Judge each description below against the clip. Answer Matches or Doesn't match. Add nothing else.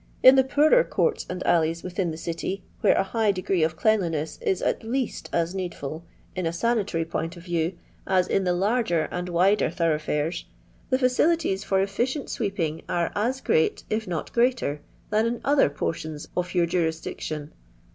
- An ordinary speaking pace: Matches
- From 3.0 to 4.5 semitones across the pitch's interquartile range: Doesn't match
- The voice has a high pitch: Doesn't match